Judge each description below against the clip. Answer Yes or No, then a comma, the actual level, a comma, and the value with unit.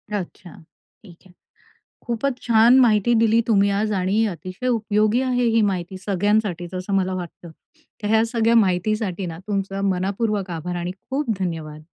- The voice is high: Yes, high, 200 Hz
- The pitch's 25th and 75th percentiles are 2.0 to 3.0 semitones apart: No, average, 3.6 semitones